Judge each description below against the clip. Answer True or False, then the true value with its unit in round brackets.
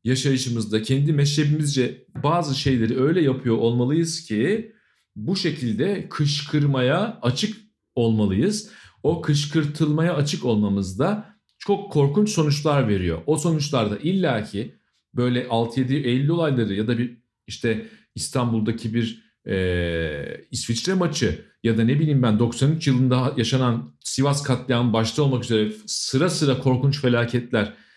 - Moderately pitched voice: False (130 Hz)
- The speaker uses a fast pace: False (120 wpm)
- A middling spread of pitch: True (4.8 semitones)